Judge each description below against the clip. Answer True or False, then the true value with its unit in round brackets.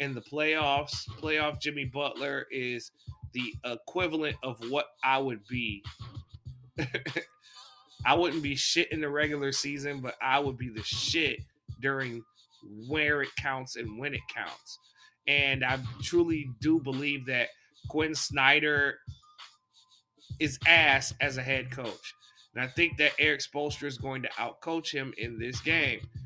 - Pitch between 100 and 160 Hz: True (135 Hz)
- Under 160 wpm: True (145 wpm)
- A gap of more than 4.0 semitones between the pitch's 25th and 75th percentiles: False (3.6 semitones)